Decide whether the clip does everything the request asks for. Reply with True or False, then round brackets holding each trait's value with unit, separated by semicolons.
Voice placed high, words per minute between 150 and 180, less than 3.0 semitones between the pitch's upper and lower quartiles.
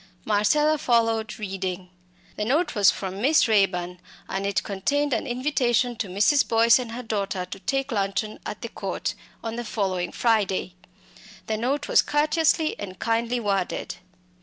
False (220 Hz; 155 wpm; 4.3 semitones)